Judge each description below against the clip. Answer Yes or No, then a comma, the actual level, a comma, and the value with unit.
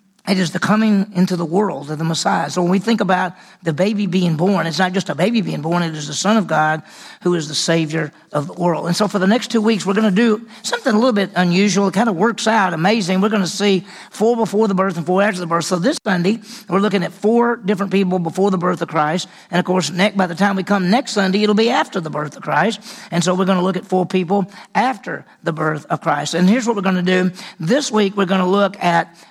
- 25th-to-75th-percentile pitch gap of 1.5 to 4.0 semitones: Yes, average, 3.0 semitones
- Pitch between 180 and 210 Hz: Yes, high, 190 Hz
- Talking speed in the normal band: No, fast, 270 wpm